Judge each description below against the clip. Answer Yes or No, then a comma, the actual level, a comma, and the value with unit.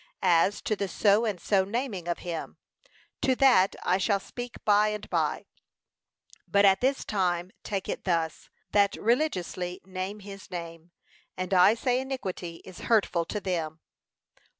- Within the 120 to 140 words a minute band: No, average, 150 wpm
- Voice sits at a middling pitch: No, high, 195 Hz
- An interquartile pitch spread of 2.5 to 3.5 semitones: Yes, average, 3.0 semitones